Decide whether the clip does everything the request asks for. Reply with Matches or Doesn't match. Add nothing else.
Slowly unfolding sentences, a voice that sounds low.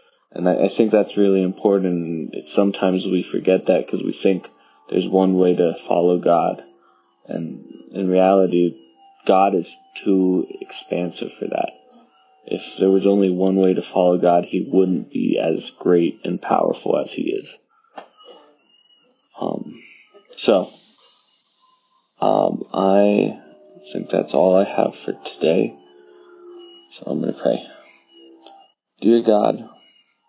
Matches